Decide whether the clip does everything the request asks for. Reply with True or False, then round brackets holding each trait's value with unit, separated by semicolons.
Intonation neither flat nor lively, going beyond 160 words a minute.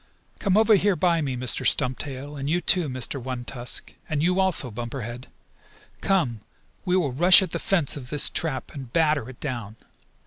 False (5.8 semitones; 185 wpm)